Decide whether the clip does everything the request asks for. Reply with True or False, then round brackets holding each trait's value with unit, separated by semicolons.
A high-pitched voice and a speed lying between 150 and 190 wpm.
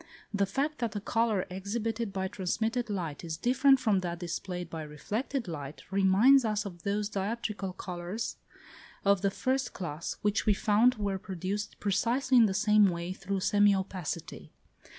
True (200 Hz; 160 wpm)